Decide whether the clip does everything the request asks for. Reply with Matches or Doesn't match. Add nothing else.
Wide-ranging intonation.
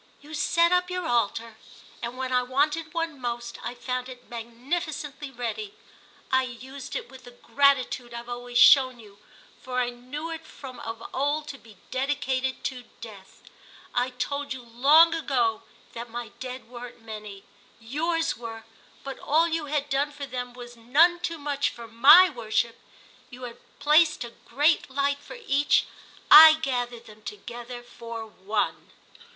Doesn't match